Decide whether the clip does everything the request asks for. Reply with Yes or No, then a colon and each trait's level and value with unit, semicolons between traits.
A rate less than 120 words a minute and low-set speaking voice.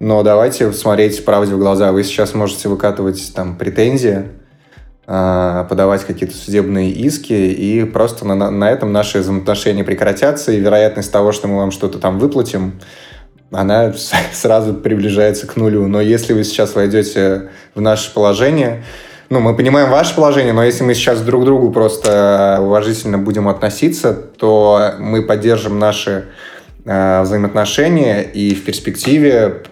No: average, 140 wpm; low, 105 Hz